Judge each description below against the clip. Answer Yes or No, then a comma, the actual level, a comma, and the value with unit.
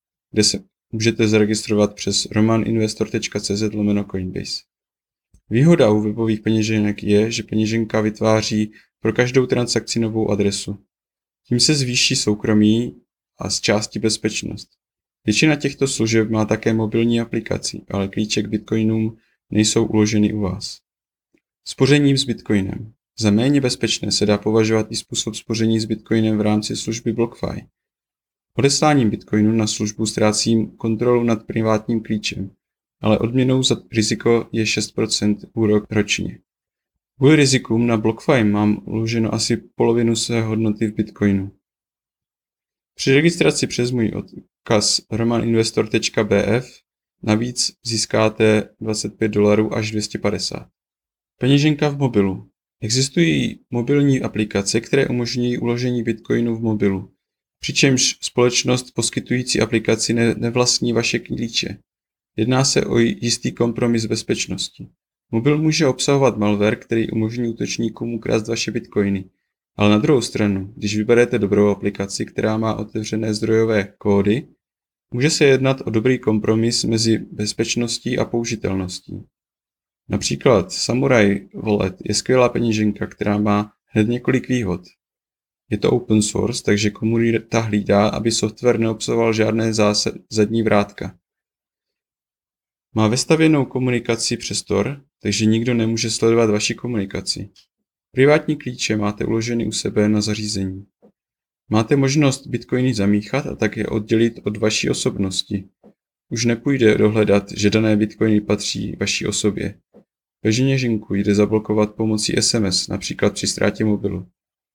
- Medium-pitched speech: No, low, 110 Hz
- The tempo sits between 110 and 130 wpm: Yes, average, 120 wpm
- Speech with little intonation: Yes, narrow, 2.0 semitones